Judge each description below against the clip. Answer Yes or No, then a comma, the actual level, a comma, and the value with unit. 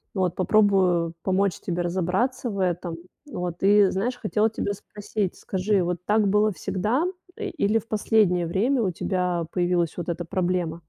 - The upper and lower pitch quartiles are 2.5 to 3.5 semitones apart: Yes, average, 3.0 semitones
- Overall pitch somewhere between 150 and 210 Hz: Yes, high, 190 Hz